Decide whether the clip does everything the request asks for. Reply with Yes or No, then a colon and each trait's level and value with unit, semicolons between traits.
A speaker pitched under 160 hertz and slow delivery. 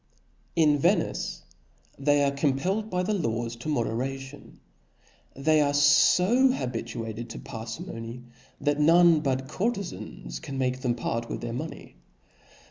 Yes: low, 135 Hz; slow, 130 wpm